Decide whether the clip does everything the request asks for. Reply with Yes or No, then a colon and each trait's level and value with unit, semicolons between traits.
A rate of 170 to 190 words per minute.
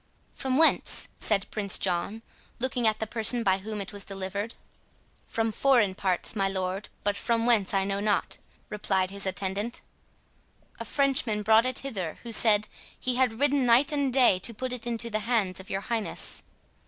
Yes: average, 180 wpm